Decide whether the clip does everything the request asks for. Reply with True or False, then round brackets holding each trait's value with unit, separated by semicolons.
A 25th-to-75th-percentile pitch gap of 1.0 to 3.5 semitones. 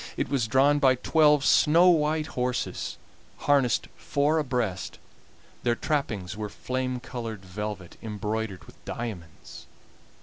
False (5.3 semitones)